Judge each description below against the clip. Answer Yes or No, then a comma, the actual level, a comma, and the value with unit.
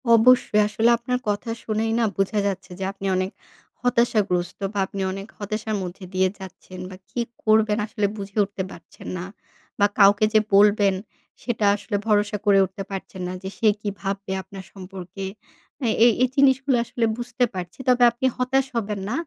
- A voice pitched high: Yes, high, 205 Hz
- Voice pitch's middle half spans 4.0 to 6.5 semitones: No, average, 2.9 semitones